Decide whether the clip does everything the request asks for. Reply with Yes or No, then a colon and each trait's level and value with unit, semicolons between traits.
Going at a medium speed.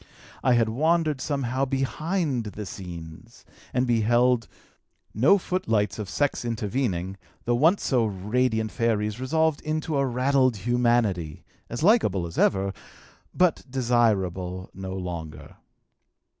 No: slow, 115 wpm